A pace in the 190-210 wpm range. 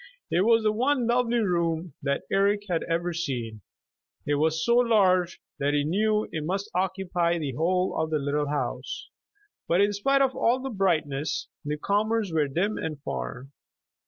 No: average, 170 wpm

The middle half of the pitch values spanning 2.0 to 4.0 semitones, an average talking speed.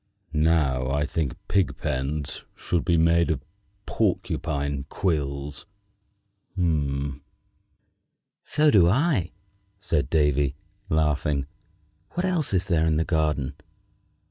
No: average, 3.3 semitones; slow, 100 wpm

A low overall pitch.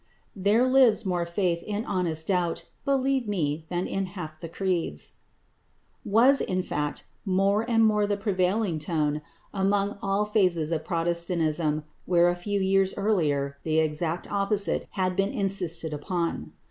No: medium, 185 Hz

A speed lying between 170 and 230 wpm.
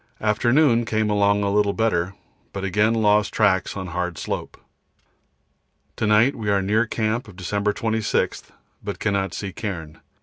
No: average, 155 wpm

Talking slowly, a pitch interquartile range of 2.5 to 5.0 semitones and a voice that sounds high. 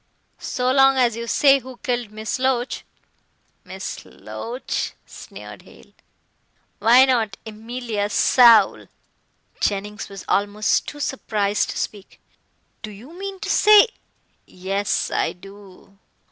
Yes: slow, 125 wpm; average, 4.0 semitones; high, 230 Hz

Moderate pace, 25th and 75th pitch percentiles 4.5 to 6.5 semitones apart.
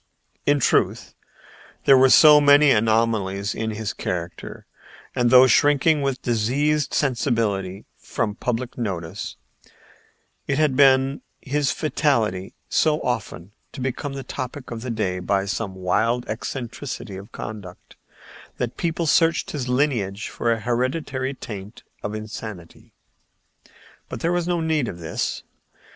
No: slow, 130 wpm; average, 5.1 semitones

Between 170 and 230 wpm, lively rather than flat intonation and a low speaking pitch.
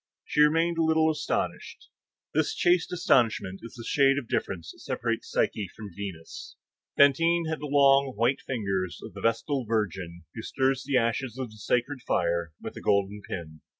Yes: average, 180 wpm; wide, 6.2 semitones; low, 120 Hz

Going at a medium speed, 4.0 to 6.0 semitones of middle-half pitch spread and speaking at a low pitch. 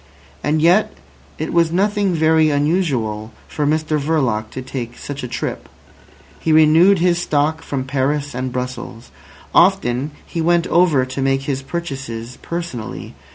No: average, 145 wpm; average, 4.4 semitones; medium, 145 Hz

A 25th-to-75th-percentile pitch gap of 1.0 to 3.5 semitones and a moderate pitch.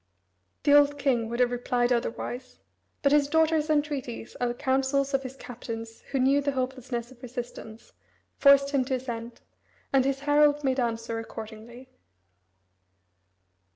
No: average, 2.7 semitones; very high, 260 Hz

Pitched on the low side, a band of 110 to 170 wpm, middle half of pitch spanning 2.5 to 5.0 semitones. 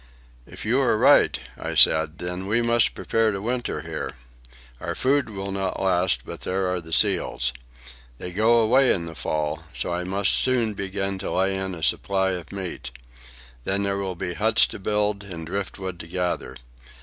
No: very low, 95 Hz; average, 185 wpm; average, 2.8 semitones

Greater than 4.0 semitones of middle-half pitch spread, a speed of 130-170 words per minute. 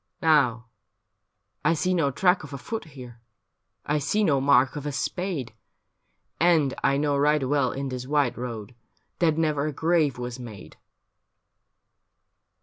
No: average, 3.7 semitones; average, 150 wpm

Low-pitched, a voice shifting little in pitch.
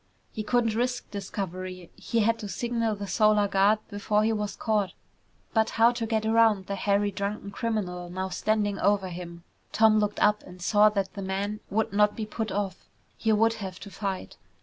No: high, 205 Hz; narrow, 2.1 semitones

